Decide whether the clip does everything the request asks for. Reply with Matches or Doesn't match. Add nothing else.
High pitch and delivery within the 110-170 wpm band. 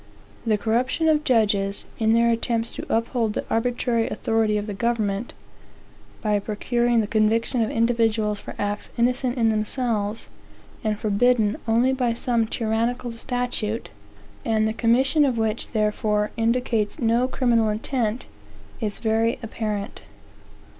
Matches